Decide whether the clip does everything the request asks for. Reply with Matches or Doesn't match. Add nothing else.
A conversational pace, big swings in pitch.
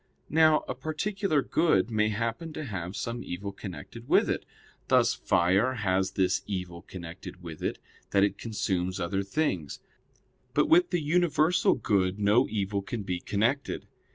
Matches